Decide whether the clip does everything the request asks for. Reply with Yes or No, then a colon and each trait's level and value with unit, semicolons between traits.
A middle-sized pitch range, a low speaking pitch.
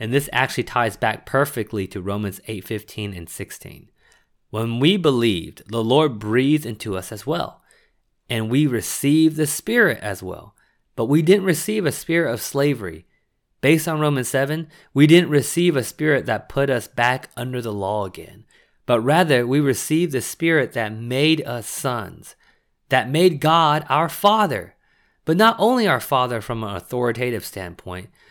No: wide, 6.0 semitones; low, 130 Hz